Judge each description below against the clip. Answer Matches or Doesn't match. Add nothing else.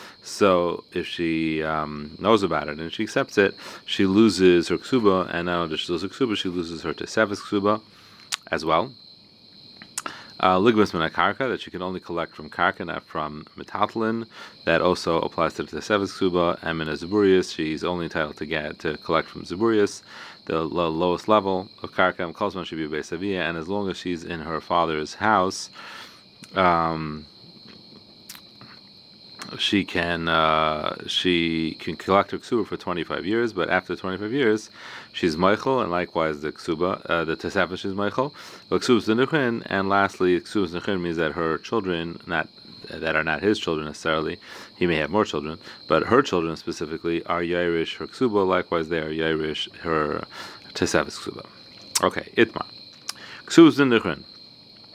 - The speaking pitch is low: Matches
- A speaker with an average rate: Matches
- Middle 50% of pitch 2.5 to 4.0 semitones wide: Matches